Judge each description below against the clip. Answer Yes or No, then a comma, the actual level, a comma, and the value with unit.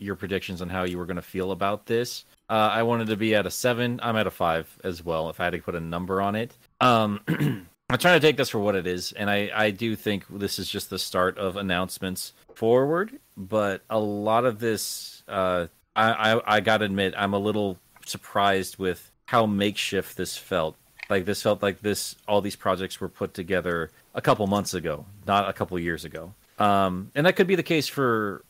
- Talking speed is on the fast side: Yes, fast, 220 wpm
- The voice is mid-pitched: No, low, 100 Hz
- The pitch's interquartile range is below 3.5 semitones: Yes, average, 2.9 semitones